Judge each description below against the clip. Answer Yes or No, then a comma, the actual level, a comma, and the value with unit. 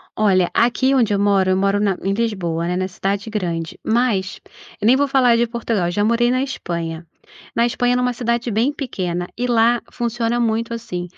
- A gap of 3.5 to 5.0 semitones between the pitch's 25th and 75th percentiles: Yes, average, 4.2 semitones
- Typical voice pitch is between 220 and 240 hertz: Yes, high, 225 Hz